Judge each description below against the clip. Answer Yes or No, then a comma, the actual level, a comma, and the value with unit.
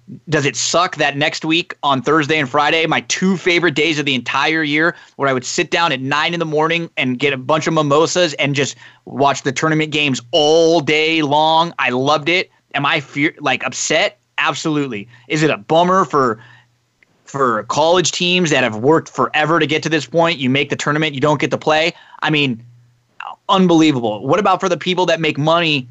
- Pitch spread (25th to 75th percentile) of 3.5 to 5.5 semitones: No, average, 2.8 semitones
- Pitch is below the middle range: No, medium, 155 Hz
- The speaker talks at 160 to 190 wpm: No, fast, 205 wpm